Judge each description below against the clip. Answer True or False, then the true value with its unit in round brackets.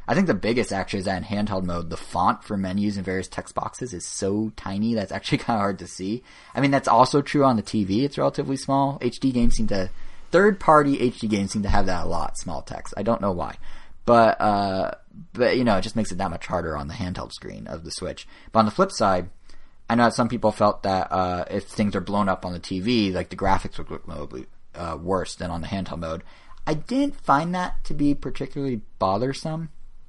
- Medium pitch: False (105 Hz)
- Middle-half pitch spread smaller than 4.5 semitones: False (4.9 semitones)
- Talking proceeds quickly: True (240 wpm)